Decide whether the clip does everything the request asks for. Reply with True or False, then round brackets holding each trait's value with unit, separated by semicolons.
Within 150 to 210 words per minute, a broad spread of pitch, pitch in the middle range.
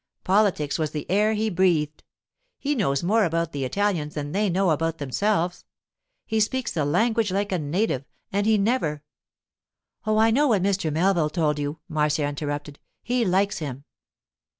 True (170 wpm; 5.7 semitones; 175 Hz)